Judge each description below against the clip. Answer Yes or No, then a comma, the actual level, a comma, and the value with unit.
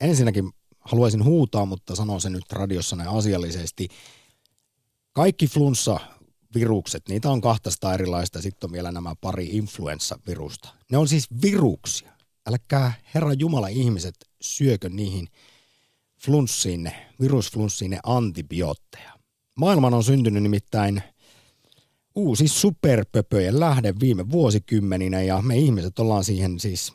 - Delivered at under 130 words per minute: Yes, average, 110 wpm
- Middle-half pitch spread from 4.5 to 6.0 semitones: Yes, wide, 5.6 semitones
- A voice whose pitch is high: No, low, 110 Hz